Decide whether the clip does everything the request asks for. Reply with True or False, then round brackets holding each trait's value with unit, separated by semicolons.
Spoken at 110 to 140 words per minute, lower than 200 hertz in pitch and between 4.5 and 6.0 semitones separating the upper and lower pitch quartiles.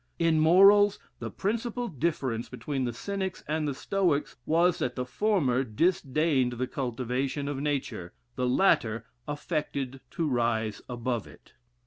True (135 wpm; 140 Hz; 5.4 semitones)